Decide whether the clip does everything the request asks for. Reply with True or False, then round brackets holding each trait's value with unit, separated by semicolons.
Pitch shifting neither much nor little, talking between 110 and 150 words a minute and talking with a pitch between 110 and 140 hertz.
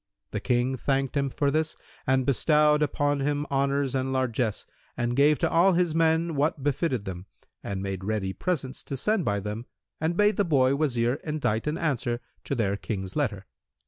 False (4.2 semitones; 180 wpm; 135 Hz)